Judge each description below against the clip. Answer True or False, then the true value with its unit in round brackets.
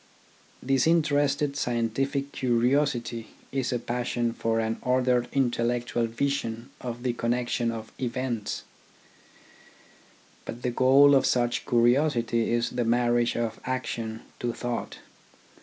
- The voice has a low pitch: True (120 Hz)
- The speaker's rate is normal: False (115 wpm)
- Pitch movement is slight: True (2.0 semitones)